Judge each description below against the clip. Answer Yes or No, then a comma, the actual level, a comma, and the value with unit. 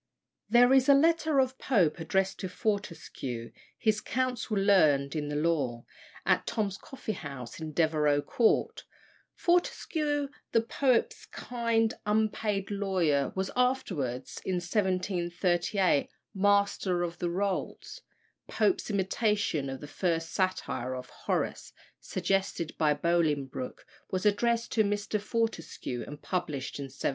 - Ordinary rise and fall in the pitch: No, wide, 6.1 semitones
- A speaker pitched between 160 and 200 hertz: Yes, high, 190 Hz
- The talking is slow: Yes, slow, 125 wpm